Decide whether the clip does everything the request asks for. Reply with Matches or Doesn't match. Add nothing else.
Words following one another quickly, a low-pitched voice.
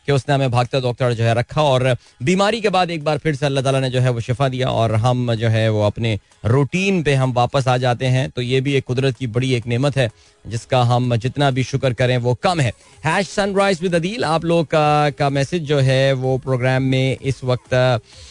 Matches